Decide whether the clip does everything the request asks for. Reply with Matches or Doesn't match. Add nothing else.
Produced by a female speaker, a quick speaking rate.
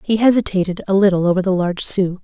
Matches